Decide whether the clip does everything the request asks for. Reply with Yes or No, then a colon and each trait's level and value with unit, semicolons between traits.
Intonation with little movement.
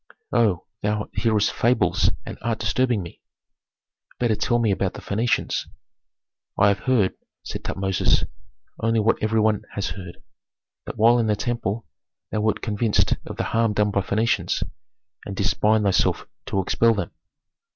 Yes: narrow, 2.3 semitones